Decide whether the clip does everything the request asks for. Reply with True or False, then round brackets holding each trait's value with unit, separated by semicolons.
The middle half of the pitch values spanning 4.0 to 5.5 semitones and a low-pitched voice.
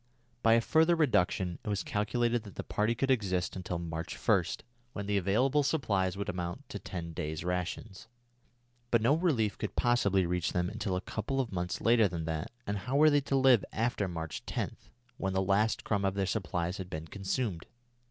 True (4.7 semitones; 100 Hz)